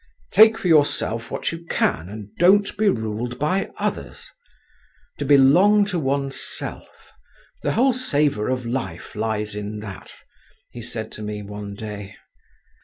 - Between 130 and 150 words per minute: Yes, slow, 135 wpm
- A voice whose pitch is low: Yes, low, 125 Hz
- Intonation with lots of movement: Yes, wide, 8.0 semitones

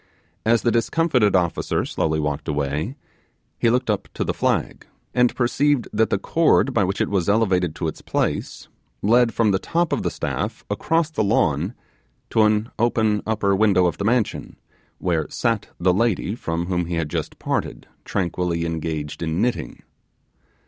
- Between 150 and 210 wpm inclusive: Yes, average, 170 wpm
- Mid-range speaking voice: No, low, 100 Hz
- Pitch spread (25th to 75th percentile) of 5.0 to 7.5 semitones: Yes, wide, 5.5 semitones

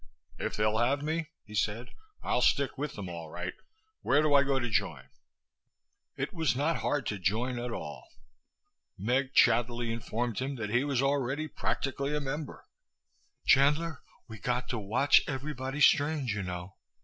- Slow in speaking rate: No, average, 160 wpm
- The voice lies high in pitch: No, low, 125 Hz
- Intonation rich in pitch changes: No, average, 4.6 semitones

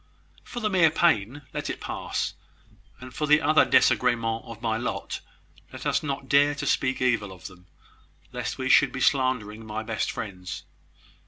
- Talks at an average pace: Yes, average, 170 wpm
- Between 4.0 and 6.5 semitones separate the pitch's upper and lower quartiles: Yes, average, 4.5 semitones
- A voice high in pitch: No, low, 125 Hz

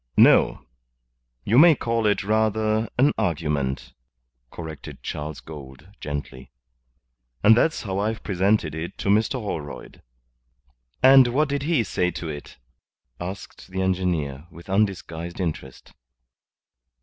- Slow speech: Yes, slow, 120 wpm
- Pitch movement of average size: No, wide, 6.0 semitones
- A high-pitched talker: No, very low, 95 Hz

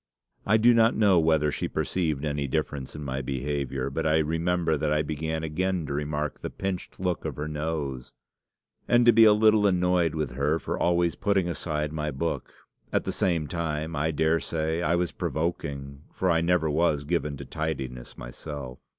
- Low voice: Yes, very low, 80 Hz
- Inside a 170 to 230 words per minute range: Yes, average, 185 wpm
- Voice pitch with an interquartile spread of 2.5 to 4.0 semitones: Yes, average, 3.1 semitones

